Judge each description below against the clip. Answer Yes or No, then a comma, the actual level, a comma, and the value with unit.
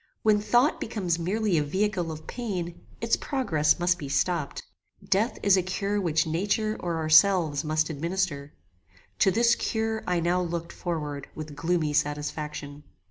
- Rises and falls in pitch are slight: No, average, 4.5 semitones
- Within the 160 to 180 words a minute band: No, average, 150 wpm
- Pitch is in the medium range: Yes, medium, 175 Hz